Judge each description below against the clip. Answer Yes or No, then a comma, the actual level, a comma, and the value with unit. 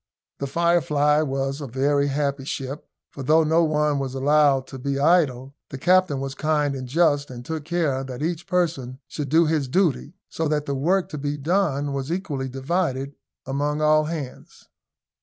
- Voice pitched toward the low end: No, medium, 145 Hz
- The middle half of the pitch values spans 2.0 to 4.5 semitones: Yes, average, 2.8 semitones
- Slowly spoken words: No, average, 175 wpm